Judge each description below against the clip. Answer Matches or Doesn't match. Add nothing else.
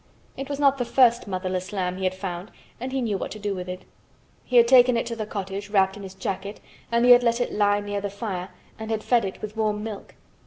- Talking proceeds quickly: Matches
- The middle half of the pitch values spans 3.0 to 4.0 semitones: Matches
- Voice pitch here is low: Doesn't match